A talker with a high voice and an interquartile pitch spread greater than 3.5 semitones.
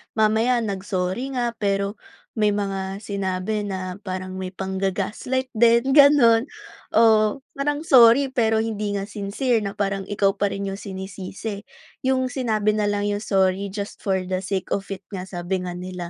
No: high, 205 Hz; average, 3.0 semitones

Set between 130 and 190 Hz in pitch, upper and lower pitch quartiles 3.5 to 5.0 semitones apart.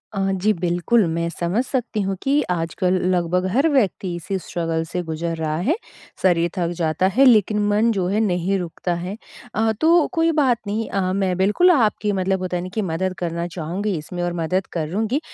Yes: medium, 185 Hz; average, 3.8 semitones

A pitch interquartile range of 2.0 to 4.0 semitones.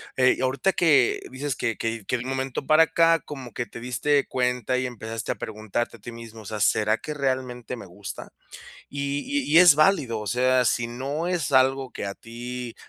Yes: average, 3.2 semitones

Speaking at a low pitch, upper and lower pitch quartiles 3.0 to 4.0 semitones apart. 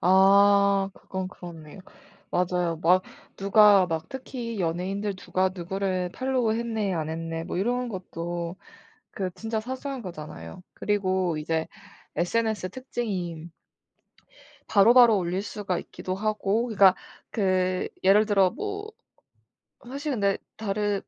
No: high, 195 Hz; average, 3.4 semitones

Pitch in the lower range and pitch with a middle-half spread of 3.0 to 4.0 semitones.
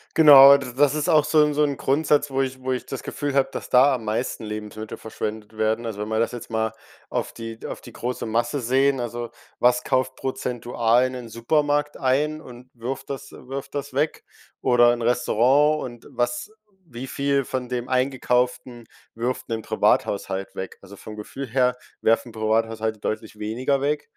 Yes: low, 125 Hz; average, 3.3 semitones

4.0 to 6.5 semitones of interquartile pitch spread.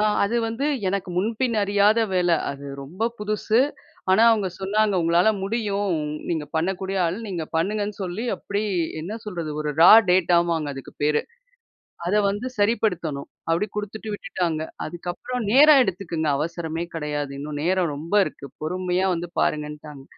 Yes: average, 4.3 semitones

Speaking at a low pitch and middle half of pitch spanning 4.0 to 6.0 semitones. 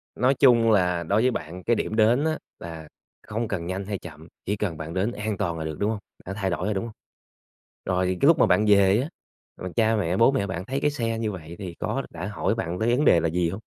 Yes: low, 100 Hz; average, 4.4 semitones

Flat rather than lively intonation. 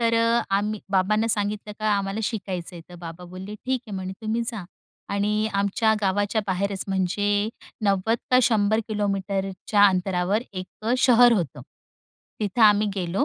Yes: narrow, 2.3 semitones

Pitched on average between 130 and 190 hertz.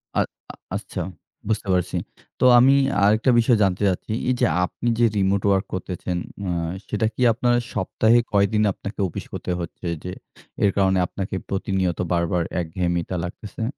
No: very low, 95 Hz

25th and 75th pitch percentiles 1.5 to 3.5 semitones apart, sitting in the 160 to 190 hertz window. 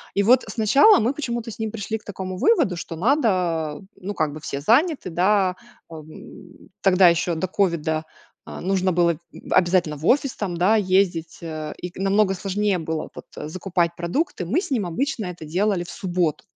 No: average, 4.0 semitones; medium, 185 Hz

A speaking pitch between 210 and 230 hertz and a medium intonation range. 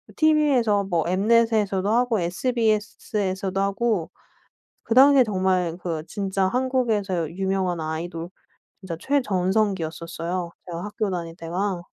No: high, 195 Hz; average, 4.2 semitones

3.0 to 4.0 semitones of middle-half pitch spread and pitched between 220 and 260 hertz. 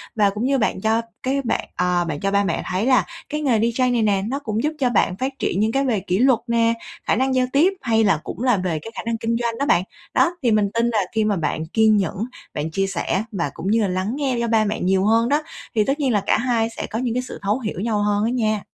Yes: average, 3.7 semitones; high, 225 Hz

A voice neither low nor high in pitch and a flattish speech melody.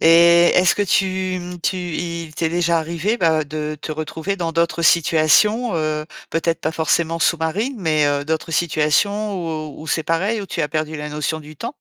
Yes: medium, 165 Hz; narrow, 2.3 semitones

